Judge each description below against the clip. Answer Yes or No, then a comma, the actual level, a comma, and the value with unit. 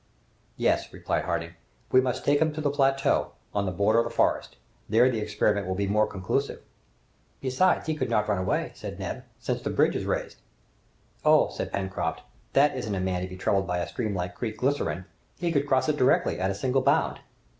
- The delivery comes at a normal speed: No, fast, 210 wpm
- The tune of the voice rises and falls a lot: Yes, wide, 5.9 semitones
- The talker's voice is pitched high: No, low, 110 Hz